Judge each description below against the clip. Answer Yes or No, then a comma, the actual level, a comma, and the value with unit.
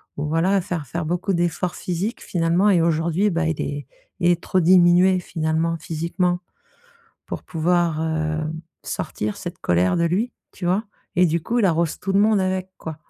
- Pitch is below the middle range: No, medium, 170 Hz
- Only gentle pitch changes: Yes, narrow, 2.3 semitones